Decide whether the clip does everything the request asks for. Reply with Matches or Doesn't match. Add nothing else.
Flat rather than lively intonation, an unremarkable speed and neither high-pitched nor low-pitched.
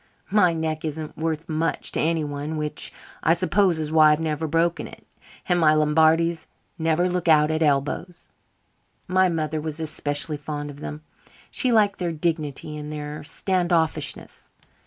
Matches